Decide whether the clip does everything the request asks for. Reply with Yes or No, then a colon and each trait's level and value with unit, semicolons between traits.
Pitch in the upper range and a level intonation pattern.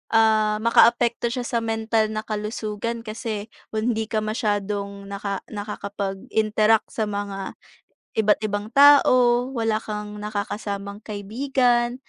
Yes: high, 215 Hz; narrow, 2.1 semitones